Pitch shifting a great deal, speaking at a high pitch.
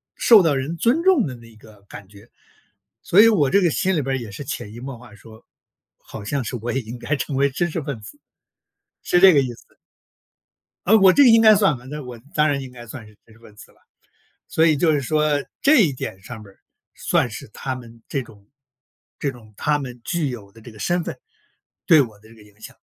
No: wide, 6.0 semitones; low, 130 Hz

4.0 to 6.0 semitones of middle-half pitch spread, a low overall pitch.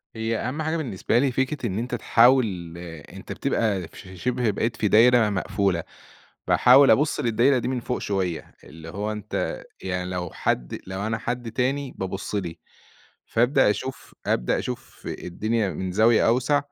Yes: average, 4.8 semitones; low, 110 Hz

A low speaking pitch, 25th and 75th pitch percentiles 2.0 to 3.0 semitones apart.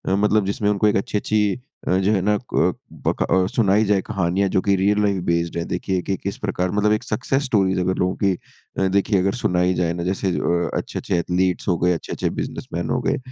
Yes: very low, 95 Hz; narrow, 2.4 semitones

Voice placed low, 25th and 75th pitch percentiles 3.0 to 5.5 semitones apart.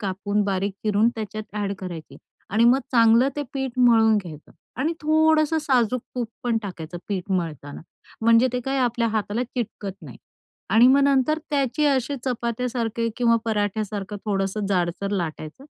No: high, 225 Hz; average, 4.1 semitones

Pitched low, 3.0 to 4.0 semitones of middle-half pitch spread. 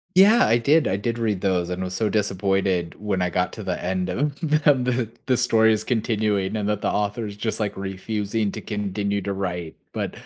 Yes: low, 105 Hz; average, 3.3 semitones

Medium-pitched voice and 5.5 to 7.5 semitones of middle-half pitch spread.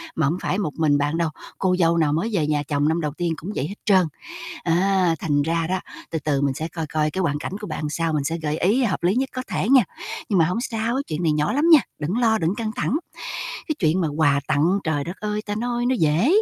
No: medium, 170 Hz; average, 5.1 semitones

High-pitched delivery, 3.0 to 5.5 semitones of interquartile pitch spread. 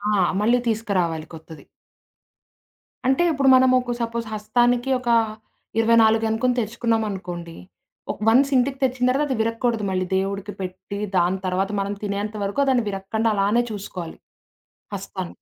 Yes: high, 220 Hz; average, 3.9 semitones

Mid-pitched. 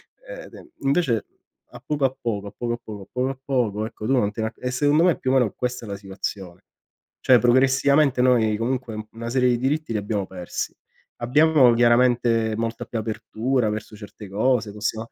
No: low, 120 Hz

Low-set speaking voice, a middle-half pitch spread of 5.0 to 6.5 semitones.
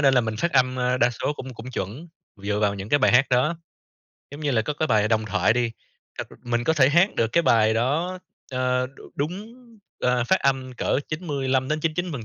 No: low, 130 Hz; average, 4.3 semitones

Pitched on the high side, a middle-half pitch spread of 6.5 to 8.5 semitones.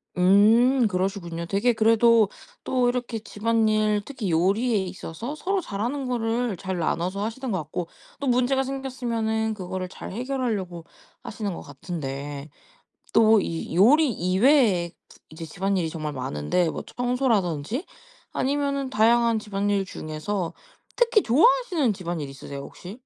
No: high, 215 Hz; wide, 5.5 semitones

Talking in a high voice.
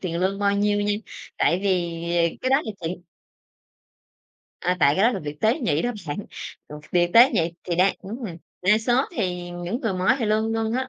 Yes: high, 195 Hz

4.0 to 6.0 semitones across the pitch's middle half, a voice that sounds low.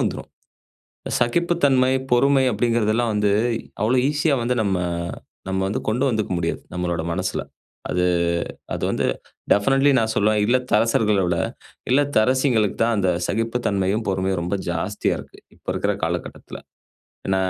Yes: average, 4.7 semitones; low, 110 Hz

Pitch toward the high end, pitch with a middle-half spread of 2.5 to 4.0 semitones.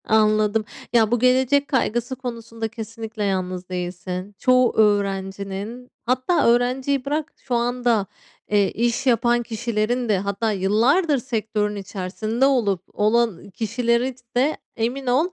Yes: high, 230 Hz; average, 3.3 semitones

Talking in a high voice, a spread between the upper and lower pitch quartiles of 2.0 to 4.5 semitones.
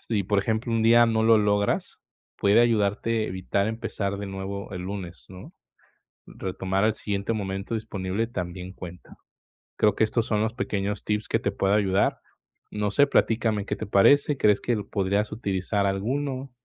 No: low, 105 Hz; narrow, 2.4 semitones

